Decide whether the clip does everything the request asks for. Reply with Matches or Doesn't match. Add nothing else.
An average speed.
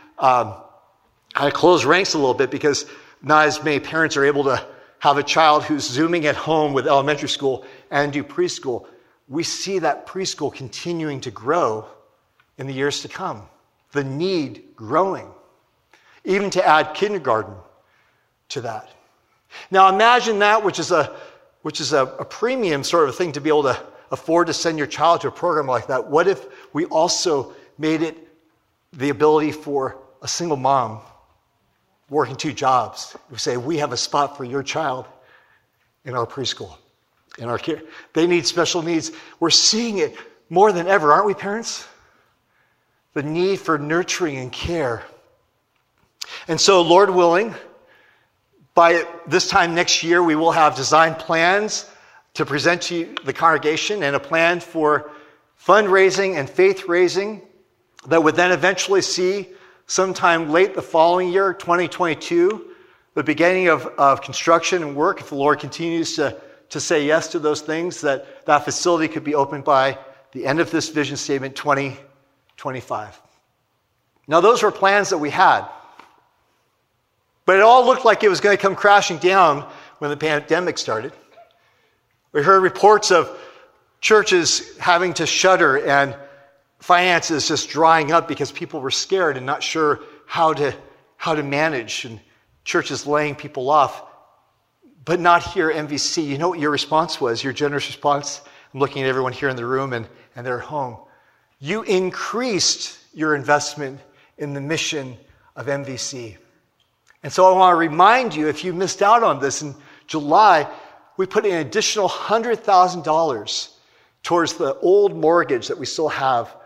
Matches